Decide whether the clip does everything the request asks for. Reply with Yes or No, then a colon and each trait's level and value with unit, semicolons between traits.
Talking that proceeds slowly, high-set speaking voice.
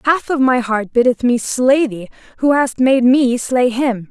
No: fast, 205 wpm; very high, 250 Hz